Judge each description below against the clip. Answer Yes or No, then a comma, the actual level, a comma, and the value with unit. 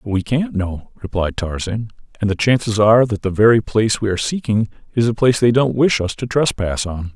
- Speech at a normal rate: No, fast, 220 wpm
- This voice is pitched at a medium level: No, low, 110 Hz